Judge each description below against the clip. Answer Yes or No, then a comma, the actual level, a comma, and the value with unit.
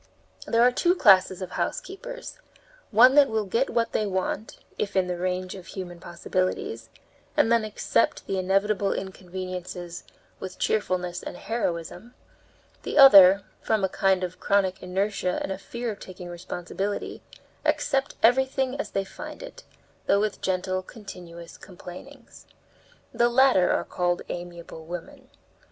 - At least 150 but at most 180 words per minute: No, average, 140 wpm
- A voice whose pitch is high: Yes, high, 195 Hz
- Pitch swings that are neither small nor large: Yes, average, 4.3 semitones